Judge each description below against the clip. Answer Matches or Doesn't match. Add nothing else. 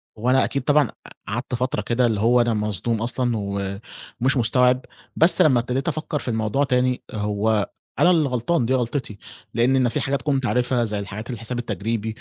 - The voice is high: Doesn't match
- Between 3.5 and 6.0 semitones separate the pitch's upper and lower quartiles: Doesn't match